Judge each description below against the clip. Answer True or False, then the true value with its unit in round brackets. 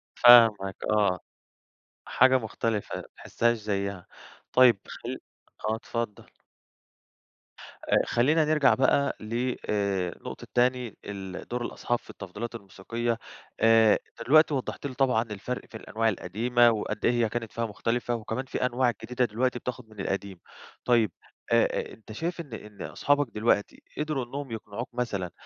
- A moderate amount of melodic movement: True (3.1 semitones)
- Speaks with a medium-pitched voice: False (115 Hz)